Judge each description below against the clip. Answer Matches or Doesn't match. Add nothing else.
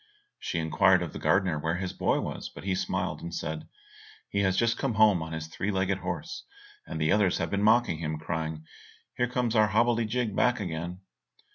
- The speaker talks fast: Matches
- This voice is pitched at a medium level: Doesn't match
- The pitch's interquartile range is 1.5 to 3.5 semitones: Doesn't match